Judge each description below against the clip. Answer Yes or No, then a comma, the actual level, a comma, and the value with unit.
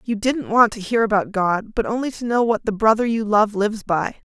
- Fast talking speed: Yes, fast, 250 wpm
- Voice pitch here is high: Yes, high, 220 Hz